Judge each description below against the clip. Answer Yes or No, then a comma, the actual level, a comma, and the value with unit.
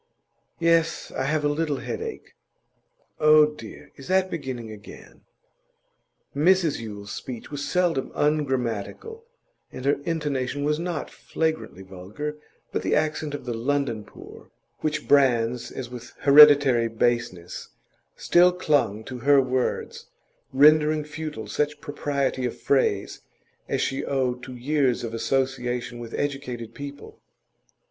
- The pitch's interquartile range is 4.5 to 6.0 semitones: No, average, 3.8 semitones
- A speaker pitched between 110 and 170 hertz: Yes, medium, 140 Hz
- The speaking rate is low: Yes, slow, 125 wpm